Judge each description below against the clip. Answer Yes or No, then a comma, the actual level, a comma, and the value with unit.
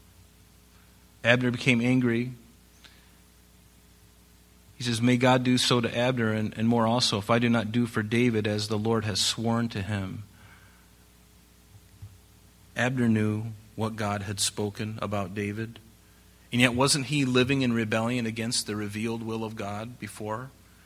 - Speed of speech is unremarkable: Yes, average, 145 wpm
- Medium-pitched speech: No, low, 110 Hz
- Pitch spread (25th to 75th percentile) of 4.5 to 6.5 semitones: No, average, 3.0 semitones